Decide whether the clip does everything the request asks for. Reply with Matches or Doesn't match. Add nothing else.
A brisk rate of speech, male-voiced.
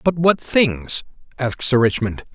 Doesn't match